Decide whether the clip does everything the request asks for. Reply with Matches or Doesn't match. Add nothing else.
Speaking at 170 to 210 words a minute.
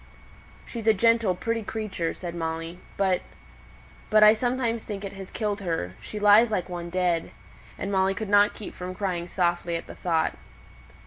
Matches